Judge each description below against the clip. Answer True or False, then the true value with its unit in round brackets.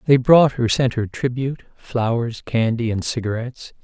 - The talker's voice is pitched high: False (120 Hz)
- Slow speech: False (155 wpm)